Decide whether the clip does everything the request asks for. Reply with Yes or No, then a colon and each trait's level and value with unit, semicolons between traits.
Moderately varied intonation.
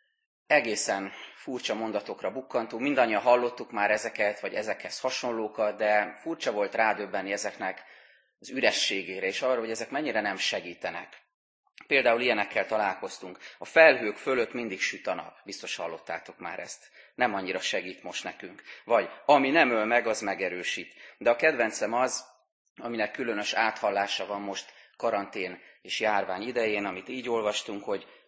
Yes: average, 3.6 semitones